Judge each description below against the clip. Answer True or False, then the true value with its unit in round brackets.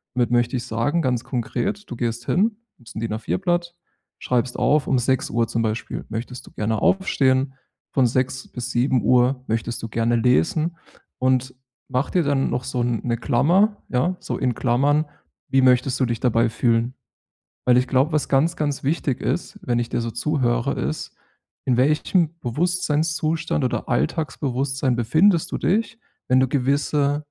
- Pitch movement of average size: True (4.0 semitones)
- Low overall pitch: True (130 Hz)